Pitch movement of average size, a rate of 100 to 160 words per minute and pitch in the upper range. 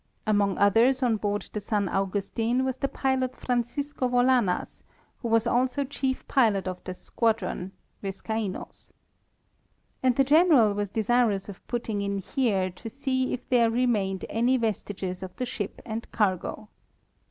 Yes: average, 4.0 semitones; average, 145 wpm; high, 225 Hz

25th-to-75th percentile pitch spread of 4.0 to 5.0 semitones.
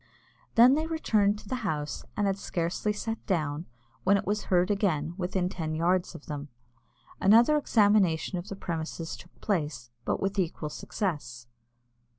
Yes: average, 4.4 semitones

